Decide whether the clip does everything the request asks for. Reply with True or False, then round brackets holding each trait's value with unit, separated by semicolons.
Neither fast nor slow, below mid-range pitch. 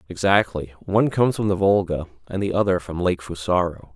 True (180 wpm; 90 Hz)